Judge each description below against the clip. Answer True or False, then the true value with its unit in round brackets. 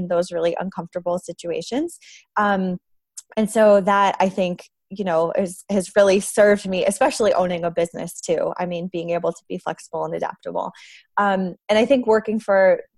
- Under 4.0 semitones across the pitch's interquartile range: True (3.2 semitones)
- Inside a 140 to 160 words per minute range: False (175 wpm)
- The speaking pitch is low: False (195 Hz)